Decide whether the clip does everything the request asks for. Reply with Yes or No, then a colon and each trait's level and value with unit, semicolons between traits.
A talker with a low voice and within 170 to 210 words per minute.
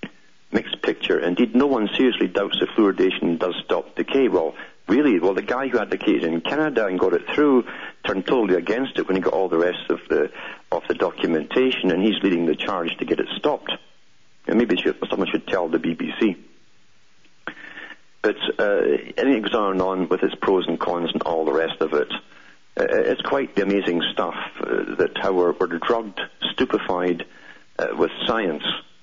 No: medium, 155 Hz; average, 190 wpm